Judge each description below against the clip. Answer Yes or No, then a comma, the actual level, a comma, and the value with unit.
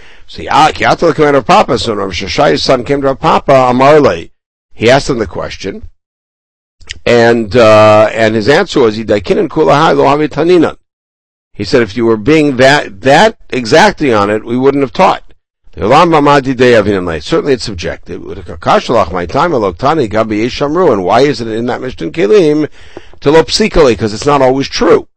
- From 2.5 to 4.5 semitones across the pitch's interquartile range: No, average, 5.3 semitones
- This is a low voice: Yes, low, 120 Hz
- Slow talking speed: Yes, slow, 125 wpm